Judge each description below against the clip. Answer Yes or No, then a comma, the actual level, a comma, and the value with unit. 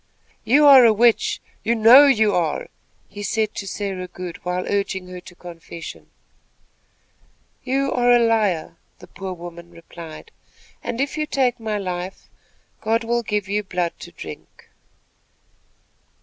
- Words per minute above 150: No, average, 145 wpm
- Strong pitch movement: No, average, 4.8 semitones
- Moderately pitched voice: No, high, 205 Hz